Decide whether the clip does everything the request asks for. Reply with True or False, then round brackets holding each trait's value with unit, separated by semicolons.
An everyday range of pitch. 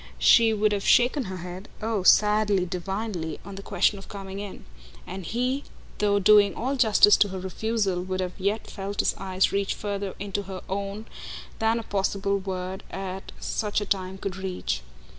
False (1.9 semitones)